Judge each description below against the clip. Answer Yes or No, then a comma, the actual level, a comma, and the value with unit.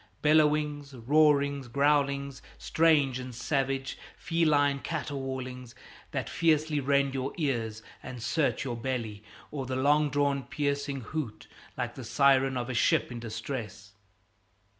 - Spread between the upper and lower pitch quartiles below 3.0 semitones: Yes, narrow, 2.4 semitones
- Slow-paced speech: Yes, slow, 125 wpm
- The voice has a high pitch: No, medium, 140 Hz